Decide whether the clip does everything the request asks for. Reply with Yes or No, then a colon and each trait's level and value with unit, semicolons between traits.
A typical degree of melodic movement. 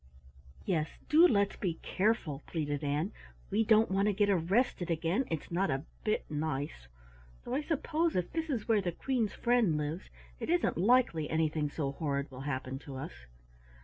No: wide, 7.0 semitones